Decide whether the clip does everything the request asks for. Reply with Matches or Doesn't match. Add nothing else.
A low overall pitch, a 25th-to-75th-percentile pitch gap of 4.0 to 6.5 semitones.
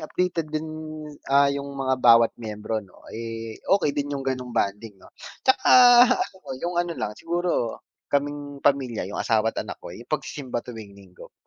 Matches